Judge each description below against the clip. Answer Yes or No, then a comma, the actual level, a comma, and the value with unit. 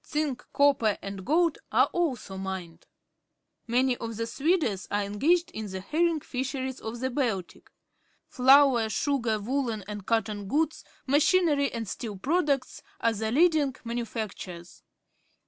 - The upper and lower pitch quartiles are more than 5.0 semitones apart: Yes, wide, 5.4 semitones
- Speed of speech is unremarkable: No, slow, 130 wpm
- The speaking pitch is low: No, high, 245 Hz